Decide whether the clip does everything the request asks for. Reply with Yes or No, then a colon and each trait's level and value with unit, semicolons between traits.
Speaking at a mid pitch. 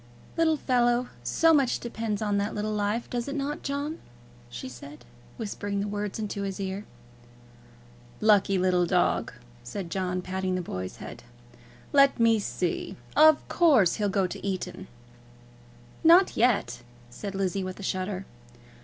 No: high, 205 Hz